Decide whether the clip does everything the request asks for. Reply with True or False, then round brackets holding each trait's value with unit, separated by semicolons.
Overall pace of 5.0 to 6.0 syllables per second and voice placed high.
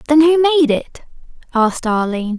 True (5.7 syllables/s; 265 Hz)